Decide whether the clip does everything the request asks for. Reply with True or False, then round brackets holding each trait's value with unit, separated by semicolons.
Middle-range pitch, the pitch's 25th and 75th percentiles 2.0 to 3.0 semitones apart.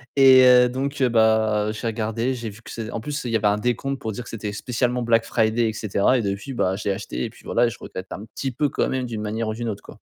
False (115 Hz; 2.5 semitones)